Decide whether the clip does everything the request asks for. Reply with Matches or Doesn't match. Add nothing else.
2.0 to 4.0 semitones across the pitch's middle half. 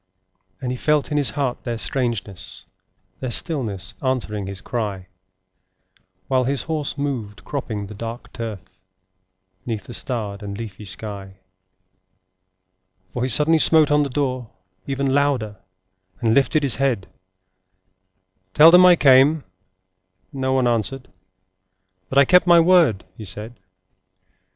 Doesn't match